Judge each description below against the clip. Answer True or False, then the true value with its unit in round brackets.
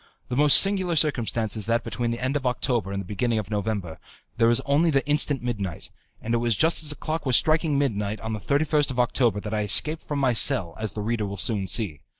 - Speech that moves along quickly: True (240 wpm)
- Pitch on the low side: True (120 Hz)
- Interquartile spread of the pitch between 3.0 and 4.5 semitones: False (5.3 semitones)